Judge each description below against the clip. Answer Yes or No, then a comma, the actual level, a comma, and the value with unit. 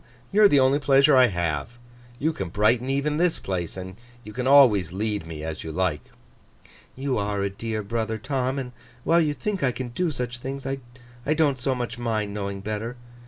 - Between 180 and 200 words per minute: Yes, average, 190 wpm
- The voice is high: No, low, 120 Hz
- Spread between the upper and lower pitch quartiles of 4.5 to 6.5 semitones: Yes, average, 5.1 semitones